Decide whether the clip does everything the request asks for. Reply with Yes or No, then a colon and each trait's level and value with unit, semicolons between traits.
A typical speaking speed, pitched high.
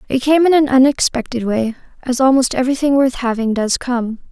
Yes: average, 180 wpm; very high, 255 Hz